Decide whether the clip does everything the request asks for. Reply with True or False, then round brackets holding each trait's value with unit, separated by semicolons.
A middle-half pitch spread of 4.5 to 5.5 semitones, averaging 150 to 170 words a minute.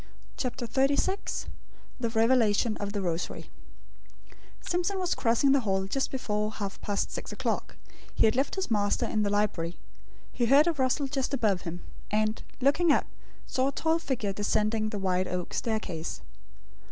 True (5.0 semitones; 160 wpm)